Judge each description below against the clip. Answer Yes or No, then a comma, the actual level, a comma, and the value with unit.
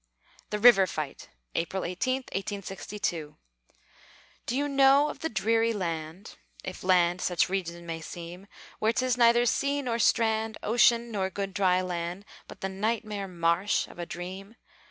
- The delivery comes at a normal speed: Yes, average, 150 wpm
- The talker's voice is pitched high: Yes, high, 195 Hz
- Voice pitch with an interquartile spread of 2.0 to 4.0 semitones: No, average, 4.5 semitones